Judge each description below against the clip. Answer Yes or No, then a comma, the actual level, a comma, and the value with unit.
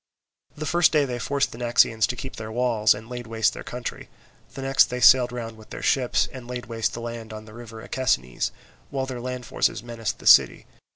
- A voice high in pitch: No, low, 120 Hz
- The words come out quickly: Yes, fast, 220 wpm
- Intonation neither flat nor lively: No, narrow, 2.1 semitones